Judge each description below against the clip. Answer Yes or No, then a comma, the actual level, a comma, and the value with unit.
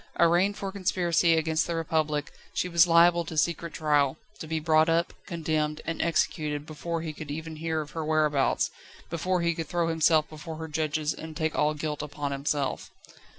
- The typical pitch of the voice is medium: Yes, medium, 160 Hz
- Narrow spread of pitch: Yes, narrow, 1.7 semitones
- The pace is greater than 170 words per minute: Yes, average, 185 wpm